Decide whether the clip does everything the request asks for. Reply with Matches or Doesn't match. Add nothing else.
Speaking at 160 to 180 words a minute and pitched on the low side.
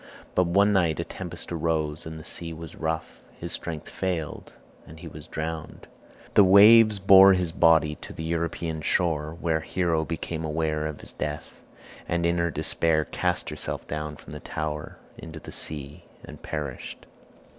Matches